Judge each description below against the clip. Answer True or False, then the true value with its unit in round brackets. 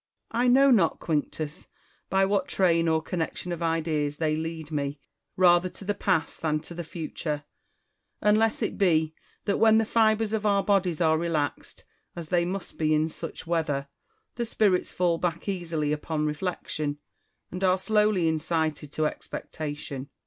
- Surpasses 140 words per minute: True (165 wpm)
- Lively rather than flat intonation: False (3.8 semitones)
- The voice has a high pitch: False (165 Hz)